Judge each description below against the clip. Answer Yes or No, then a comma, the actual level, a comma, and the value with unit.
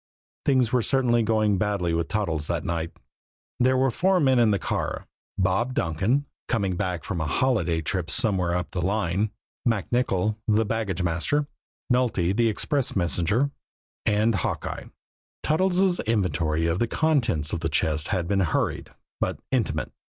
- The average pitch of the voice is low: Yes, low, 105 Hz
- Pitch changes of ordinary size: No, wide, 5.8 semitones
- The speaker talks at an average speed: Yes, average, 150 wpm